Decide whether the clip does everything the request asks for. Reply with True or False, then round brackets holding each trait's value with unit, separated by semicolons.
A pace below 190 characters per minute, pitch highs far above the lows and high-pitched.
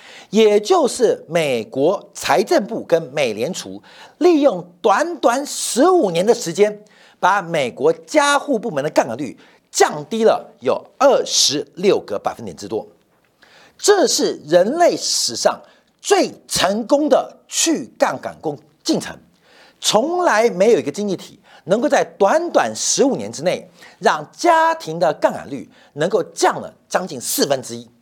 False (210 characters per minute; 8.9 semitones; 285 Hz)